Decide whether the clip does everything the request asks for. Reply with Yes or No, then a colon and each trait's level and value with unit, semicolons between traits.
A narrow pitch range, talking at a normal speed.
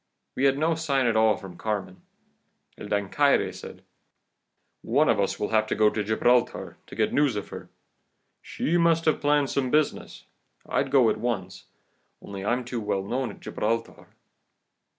No: average, 4.8 semitones; average, 170 wpm